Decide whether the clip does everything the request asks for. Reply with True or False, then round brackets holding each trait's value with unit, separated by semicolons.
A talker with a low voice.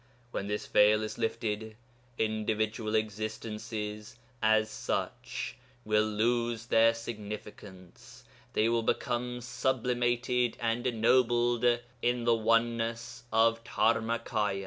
True (115 Hz)